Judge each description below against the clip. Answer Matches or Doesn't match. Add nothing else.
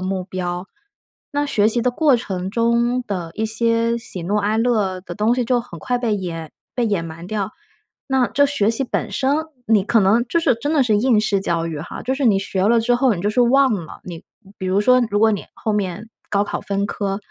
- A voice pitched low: Doesn't match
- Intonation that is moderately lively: Matches